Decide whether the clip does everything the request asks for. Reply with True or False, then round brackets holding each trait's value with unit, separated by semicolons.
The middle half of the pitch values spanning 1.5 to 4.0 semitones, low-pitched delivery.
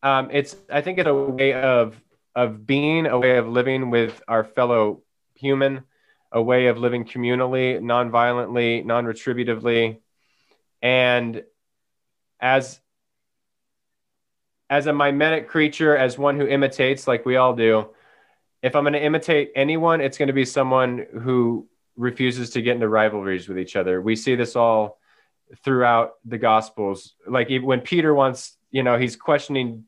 True (2.7 semitones; 125 Hz)